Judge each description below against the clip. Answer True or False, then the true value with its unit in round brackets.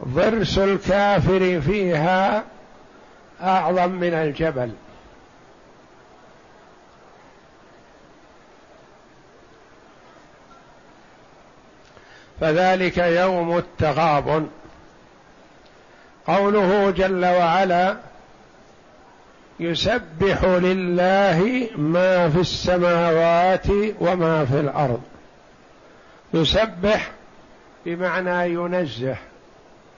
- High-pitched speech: False (180 Hz)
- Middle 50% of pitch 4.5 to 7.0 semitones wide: False (2.4 semitones)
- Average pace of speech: False (45 wpm)